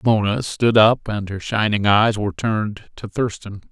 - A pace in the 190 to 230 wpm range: No, average, 180 wpm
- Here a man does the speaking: Yes, male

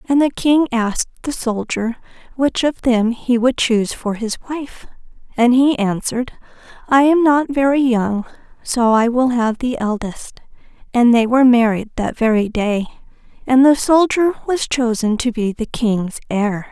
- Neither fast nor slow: Yes, average, 160 wpm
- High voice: Yes, high, 240 Hz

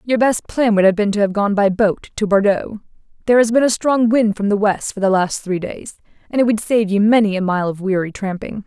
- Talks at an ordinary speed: No, fast, 265 wpm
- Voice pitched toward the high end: Yes, high, 210 Hz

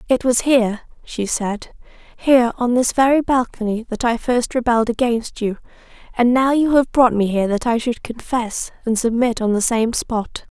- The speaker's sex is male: No, female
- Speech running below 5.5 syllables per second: Yes, 5.0 syllables/s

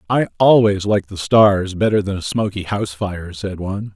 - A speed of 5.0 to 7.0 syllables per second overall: Yes, 5.2 syllables/s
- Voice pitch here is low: Yes, low, 100 Hz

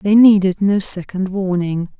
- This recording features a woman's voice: Yes, female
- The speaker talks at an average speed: Yes, average, 150 wpm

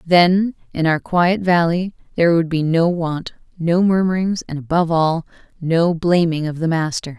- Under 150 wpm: No, average, 165 wpm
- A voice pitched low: No, medium, 170 Hz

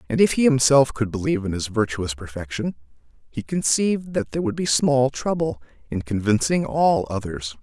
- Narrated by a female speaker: No, male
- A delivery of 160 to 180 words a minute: Yes, average, 175 wpm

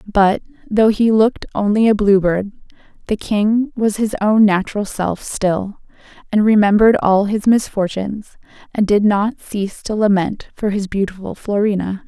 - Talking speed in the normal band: Yes, average, 155 wpm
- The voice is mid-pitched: No, high, 205 Hz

